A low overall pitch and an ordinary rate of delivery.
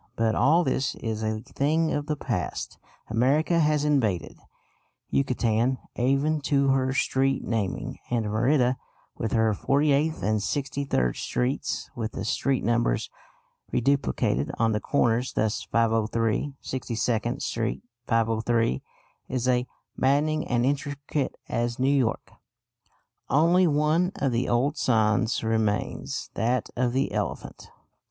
No: low, 125 Hz; slow, 125 wpm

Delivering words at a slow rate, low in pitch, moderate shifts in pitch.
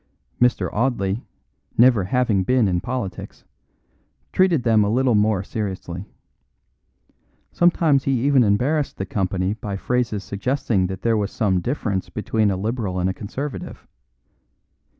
Yes: slow, 130 wpm; low, 110 Hz; average, 4.7 semitones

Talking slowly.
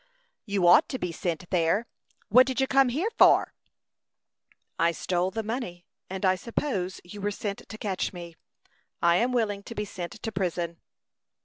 No: average, 175 wpm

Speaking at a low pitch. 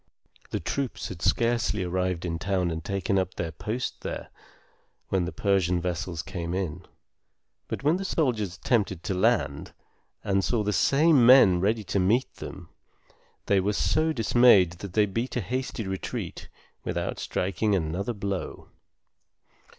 Yes: low, 100 Hz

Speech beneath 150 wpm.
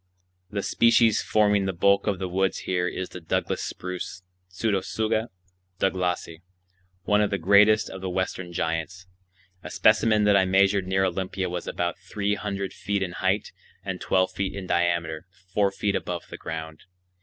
No: average, 165 wpm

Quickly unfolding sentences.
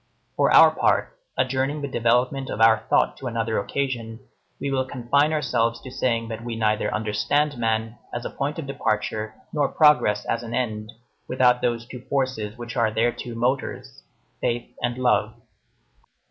No: average, 165 wpm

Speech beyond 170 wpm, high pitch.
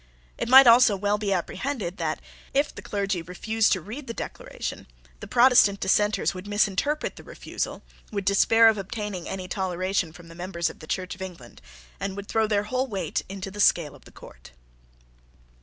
Yes: average, 185 wpm; high, 200 Hz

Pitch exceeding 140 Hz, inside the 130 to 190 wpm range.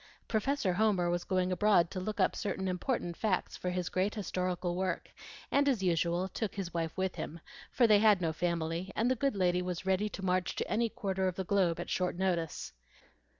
No: medium, 185 Hz; fast, 205 wpm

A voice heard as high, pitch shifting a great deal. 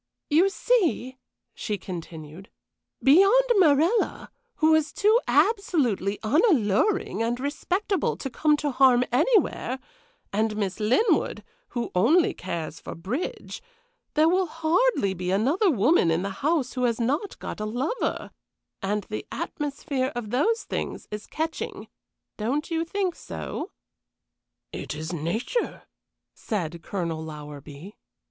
Yes: very high, 255 Hz; wide, 8.8 semitones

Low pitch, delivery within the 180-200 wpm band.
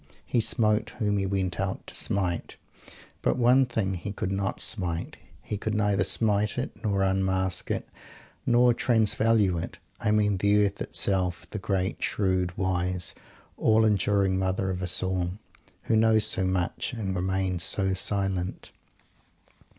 No: very low, 95 Hz; average, 150 wpm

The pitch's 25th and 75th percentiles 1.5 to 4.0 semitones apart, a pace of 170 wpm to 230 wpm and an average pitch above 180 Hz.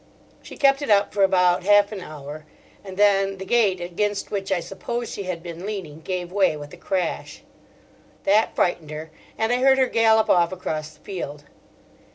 Yes: average, 3.3 semitones; average, 190 wpm; high, 190 Hz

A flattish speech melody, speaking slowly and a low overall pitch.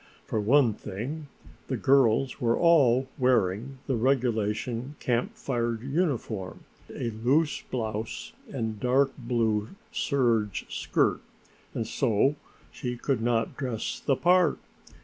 No: average, 3.5 semitones; slow, 115 wpm; low, 120 Hz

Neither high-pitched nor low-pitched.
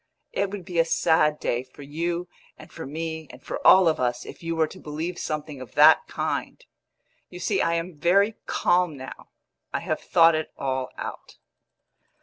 Yes: medium, 160 Hz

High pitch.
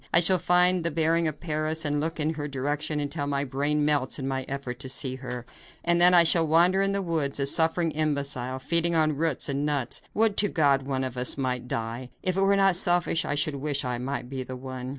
No: medium, 150 Hz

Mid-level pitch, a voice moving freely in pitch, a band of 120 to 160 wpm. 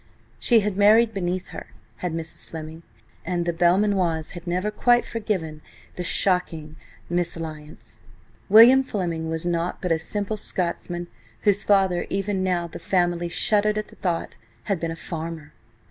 No: medium, 175 Hz; average, 3.6 semitones; average, 145 wpm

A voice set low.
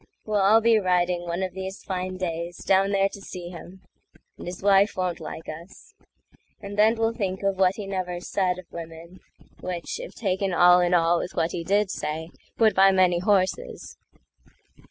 No: medium, 185 Hz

